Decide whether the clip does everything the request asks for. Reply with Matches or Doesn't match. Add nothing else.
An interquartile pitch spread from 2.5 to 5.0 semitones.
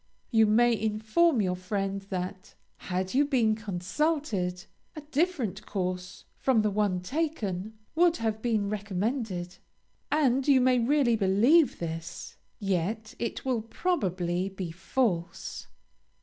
Doesn't match